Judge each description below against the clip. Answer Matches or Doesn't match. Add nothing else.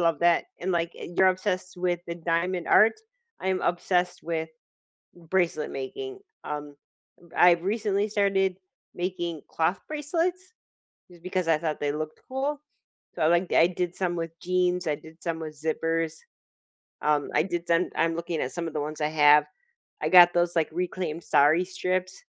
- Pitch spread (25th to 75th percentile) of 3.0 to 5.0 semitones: Doesn't match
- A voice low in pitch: Doesn't match